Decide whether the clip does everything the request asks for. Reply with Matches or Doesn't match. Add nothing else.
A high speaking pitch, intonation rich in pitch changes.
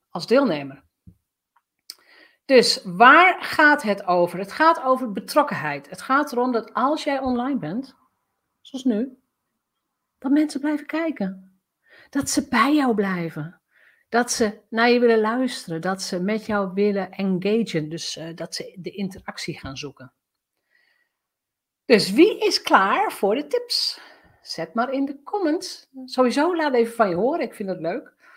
Matches